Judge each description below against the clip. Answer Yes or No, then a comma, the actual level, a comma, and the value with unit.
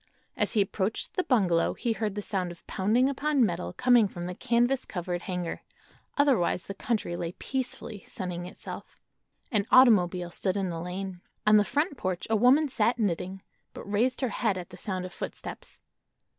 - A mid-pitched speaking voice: No, high, 200 Hz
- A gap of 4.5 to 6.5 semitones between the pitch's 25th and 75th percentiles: Yes, average, 5.1 semitones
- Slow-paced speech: No, average, 180 wpm